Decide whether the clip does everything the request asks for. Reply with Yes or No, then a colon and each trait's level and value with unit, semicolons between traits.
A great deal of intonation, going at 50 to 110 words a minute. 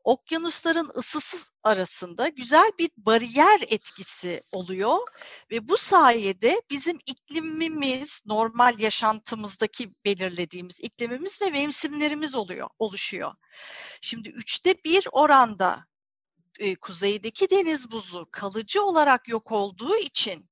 Yes: wide, 7.0 semitones; average, 100 wpm